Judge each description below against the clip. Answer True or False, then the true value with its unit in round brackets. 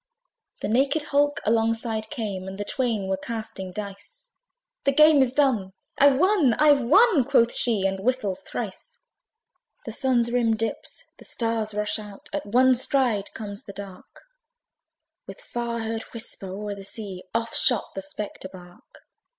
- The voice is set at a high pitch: True (225 Hz)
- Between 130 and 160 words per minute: True (155 wpm)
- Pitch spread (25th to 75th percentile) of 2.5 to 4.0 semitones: False (4.4 semitones)